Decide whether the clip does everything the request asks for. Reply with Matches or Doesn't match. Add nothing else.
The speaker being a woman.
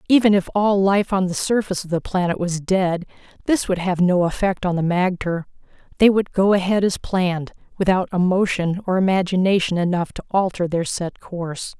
Matches